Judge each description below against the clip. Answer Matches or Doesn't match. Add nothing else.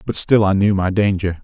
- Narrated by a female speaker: Doesn't match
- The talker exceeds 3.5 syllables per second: Matches